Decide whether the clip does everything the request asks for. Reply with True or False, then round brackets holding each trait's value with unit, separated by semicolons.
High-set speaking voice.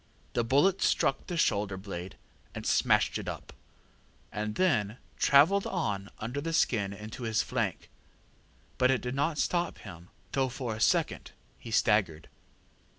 False (115 Hz)